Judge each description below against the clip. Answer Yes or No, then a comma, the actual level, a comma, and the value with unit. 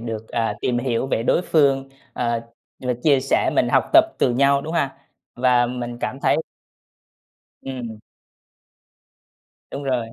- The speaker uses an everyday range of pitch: No, narrow, 2.3 semitones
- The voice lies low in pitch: Yes, low, 125 Hz